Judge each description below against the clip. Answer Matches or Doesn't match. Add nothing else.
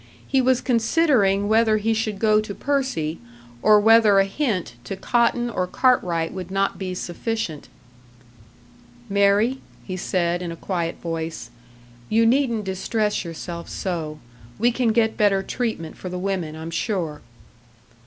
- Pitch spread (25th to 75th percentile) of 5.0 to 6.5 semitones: Doesn't match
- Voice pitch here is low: Doesn't match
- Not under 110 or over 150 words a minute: Matches